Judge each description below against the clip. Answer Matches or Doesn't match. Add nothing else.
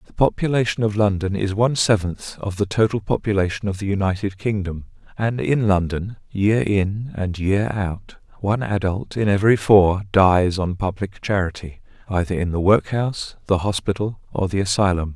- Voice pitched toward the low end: Matches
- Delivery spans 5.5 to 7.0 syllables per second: Doesn't match